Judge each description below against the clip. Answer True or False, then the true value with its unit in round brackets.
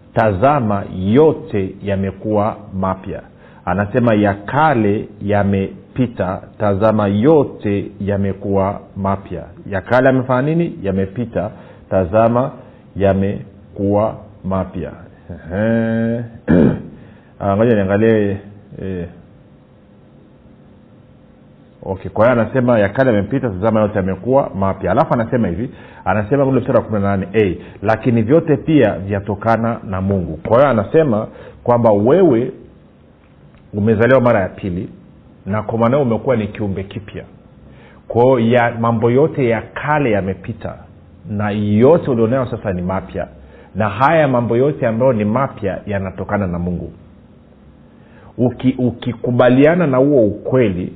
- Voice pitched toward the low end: True (105 Hz)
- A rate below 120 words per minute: True (105 wpm)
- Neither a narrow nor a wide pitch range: True (3.7 semitones)